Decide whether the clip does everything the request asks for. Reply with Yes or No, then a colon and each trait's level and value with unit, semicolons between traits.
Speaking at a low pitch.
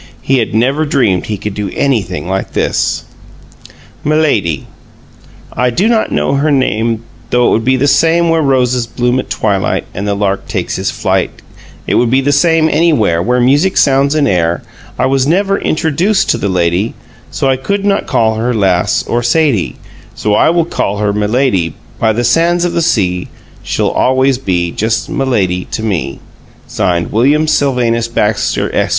Yes: low, 125 Hz